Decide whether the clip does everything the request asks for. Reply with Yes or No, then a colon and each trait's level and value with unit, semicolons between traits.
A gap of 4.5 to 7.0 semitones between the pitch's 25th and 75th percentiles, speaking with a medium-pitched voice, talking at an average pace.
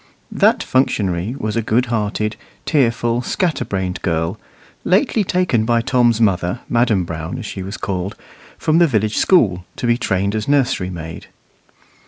No: average, 5.0 semitones; low, 110 Hz; average, 150 wpm